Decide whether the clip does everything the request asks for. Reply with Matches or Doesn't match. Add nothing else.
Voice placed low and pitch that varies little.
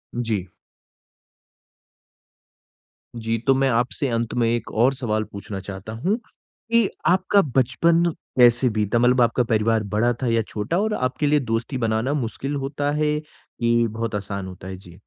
Doesn't match